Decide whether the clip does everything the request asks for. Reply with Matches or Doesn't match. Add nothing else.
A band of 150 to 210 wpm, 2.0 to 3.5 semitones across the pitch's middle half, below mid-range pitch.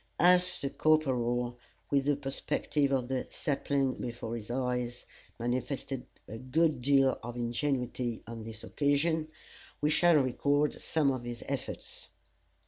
Doesn't match